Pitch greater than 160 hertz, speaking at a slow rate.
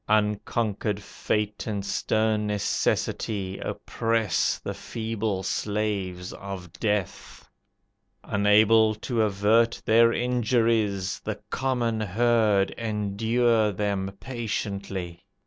No: low, 105 Hz; slow, 85 wpm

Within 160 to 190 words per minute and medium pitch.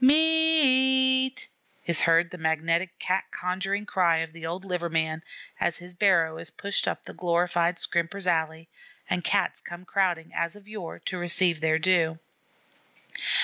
Yes: average, 165 wpm; medium, 175 Hz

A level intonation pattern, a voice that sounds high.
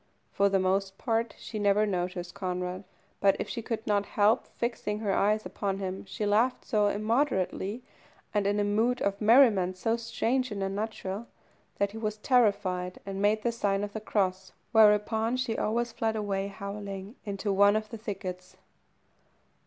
Yes: narrow, 2.3 semitones; high, 205 Hz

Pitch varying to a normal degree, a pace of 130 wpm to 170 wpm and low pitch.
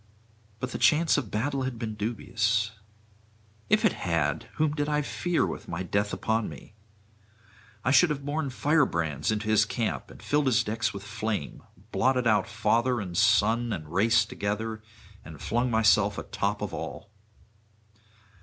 Yes: average, 3.9 semitones; average, 160 wpm; low, 115 Hz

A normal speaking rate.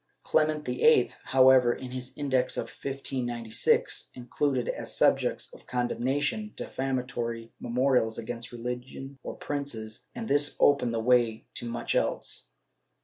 No: slow, 130 wpm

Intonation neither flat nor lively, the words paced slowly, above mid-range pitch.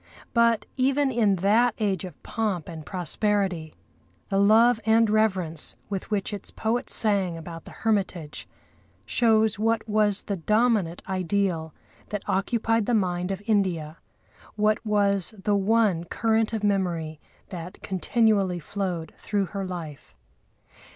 Yes: average, 3.5 semitones; slow, 130 wpm; high, 200 Hz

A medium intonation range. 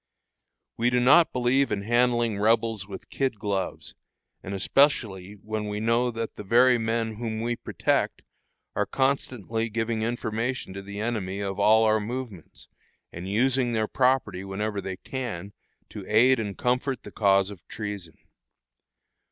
Yes: average, 3.3 semitones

